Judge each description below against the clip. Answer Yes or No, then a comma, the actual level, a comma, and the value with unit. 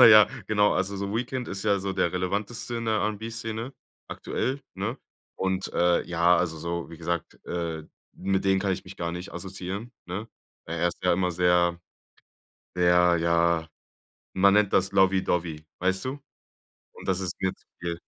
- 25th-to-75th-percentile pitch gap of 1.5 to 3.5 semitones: Yes, average, 2.9 semitones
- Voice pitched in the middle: No, very low, 95 Hz